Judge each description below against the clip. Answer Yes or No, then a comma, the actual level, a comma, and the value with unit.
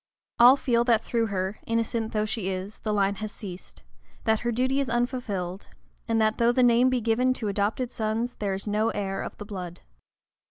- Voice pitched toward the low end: No, high, 220 Hz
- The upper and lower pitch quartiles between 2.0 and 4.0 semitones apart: Yes, average, 2.9 semitones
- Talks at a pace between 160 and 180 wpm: No, average, 200 wpm